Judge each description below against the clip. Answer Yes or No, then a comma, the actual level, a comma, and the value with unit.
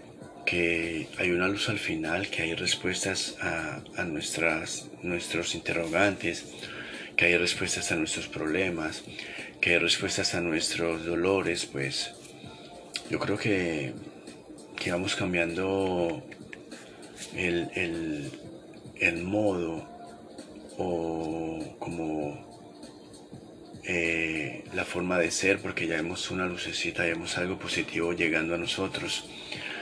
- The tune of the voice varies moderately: No, narrow, 1.8 semitones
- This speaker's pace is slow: Yes, slow, 115 wpm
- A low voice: Yes, very low, 85 Hz